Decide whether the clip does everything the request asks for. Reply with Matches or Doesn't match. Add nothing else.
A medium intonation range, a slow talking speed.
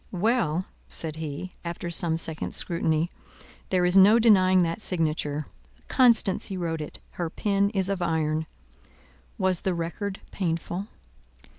Matches